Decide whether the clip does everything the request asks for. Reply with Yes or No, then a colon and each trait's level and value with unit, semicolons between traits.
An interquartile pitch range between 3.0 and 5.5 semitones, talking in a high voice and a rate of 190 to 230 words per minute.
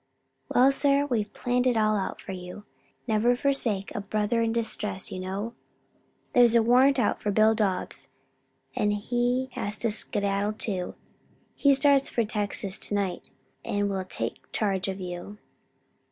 No: average, 3.4 semitones; high, 215 Hz; average, 155 wpm